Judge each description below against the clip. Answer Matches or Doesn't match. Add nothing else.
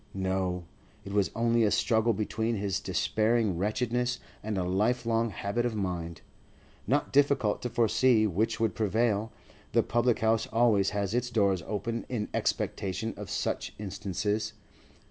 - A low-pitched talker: Matches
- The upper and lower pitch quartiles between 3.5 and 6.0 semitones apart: Doesn't match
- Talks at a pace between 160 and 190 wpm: Doesn't match